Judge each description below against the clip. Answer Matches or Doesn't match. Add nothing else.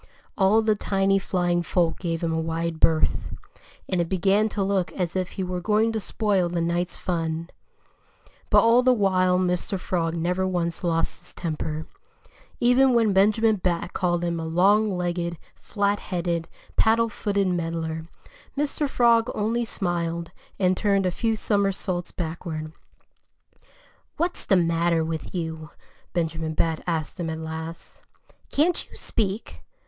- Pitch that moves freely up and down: Doesn't match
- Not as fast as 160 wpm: Matches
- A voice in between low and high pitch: Matches